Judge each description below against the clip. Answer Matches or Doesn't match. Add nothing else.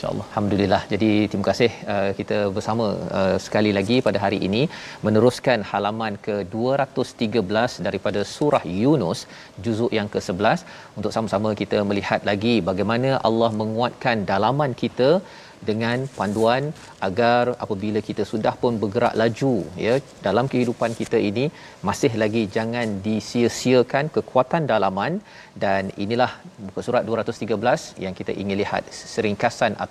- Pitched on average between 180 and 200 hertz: Doesn't match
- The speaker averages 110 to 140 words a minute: Matches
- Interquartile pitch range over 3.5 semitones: Doesn't match